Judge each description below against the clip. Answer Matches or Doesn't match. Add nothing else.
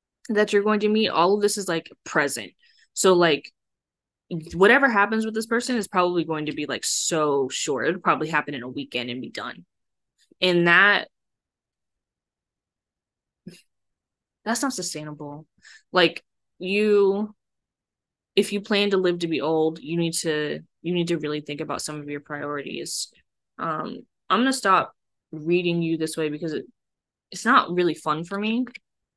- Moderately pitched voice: Matches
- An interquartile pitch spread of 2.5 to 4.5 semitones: Doesn't match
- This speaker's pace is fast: Doesn't match